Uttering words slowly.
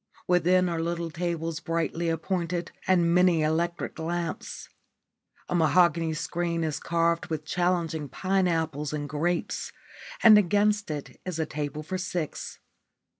Yes: slow, 130 wpm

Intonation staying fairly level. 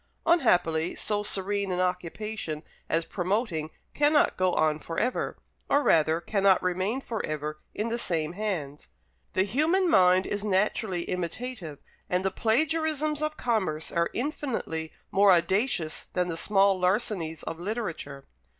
No: average, 5.1 semitones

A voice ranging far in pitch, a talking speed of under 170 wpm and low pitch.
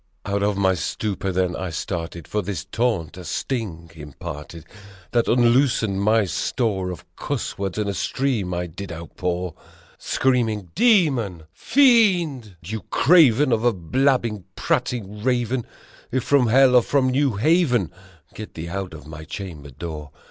Yes: wide, 6.0 semitones; average, 145 wpm; low, 105 Hz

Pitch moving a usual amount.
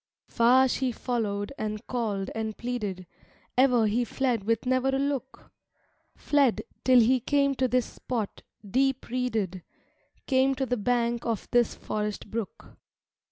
Yes: average, 3.1 semitones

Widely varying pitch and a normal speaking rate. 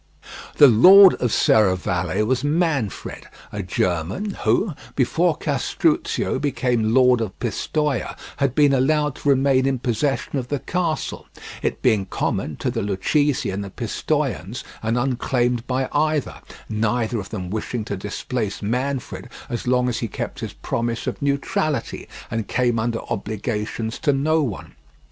No: average, 4.6 semitones; average, 145 wpm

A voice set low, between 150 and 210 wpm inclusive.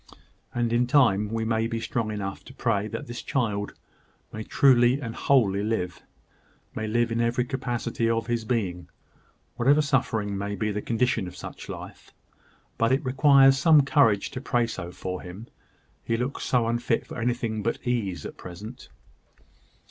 Yes: low, 115 Hz; average, 165 wpm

